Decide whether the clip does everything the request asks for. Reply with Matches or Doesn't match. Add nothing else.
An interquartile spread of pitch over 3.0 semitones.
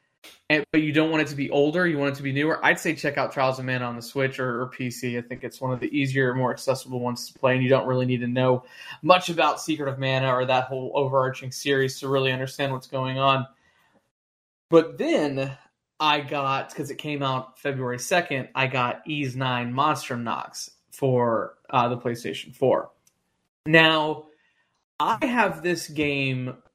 Doesn't match